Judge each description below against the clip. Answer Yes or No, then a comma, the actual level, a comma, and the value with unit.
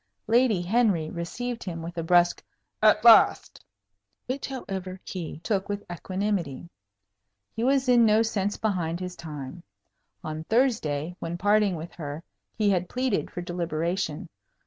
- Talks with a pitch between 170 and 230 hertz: Yes, medium, 185 Hz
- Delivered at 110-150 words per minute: Yes, average, 140 wpm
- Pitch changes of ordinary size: Yes, average, 4.5 semitones